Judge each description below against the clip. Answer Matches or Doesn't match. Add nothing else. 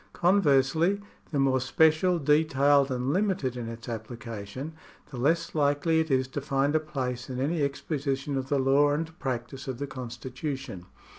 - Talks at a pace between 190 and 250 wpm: Doesn't match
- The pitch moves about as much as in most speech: Matches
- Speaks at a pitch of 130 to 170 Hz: Matches